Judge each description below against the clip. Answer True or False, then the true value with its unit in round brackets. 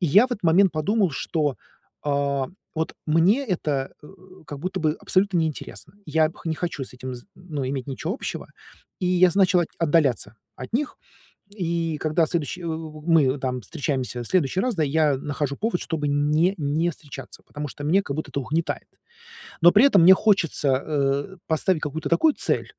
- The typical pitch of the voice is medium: True (160 Hz)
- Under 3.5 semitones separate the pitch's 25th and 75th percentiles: False (4.0 semitones)